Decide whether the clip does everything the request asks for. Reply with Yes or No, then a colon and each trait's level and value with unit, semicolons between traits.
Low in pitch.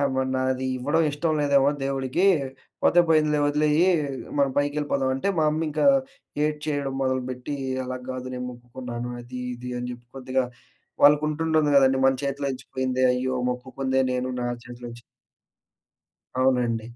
Yes: low, 130 Hz